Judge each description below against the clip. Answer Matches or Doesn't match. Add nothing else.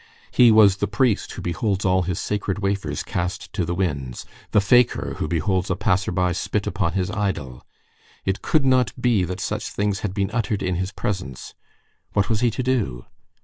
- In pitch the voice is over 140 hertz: Doesn't match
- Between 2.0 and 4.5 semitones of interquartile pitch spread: Matches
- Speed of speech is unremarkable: Matches